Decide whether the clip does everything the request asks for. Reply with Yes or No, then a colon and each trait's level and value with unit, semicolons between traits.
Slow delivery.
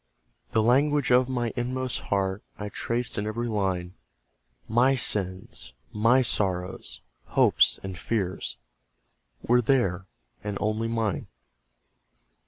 Yes: slow, 110 wpm